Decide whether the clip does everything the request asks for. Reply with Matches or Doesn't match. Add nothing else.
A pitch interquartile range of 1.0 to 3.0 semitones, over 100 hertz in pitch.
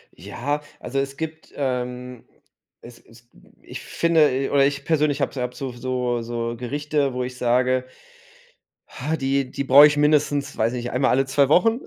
Matches